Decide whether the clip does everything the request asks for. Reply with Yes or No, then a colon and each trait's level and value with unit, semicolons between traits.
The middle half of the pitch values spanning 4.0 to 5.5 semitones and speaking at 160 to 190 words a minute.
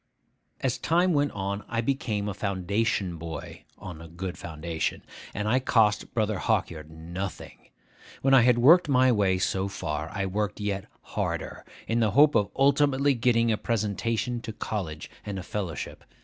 Yes: average, 4.6 semitones; average, 165 wpm